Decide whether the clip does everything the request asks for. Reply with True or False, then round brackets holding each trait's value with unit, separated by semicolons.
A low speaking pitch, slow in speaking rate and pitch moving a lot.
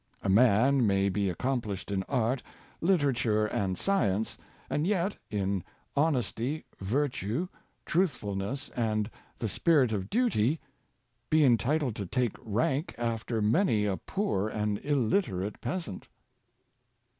True (115 Hz; 120 wpm; 5.9 semitones)